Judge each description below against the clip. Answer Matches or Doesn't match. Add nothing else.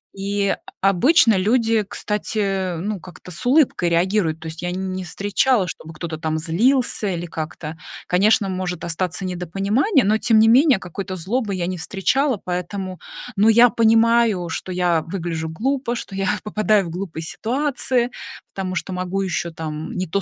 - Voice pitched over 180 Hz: Matches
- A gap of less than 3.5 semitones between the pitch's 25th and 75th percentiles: Doesn't match